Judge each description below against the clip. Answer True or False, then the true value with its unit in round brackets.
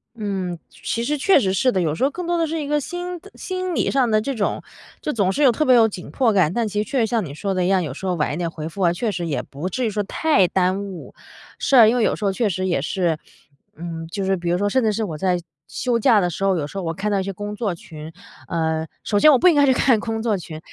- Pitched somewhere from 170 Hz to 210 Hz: True (200 Hz)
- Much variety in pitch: True (5.8 semitones)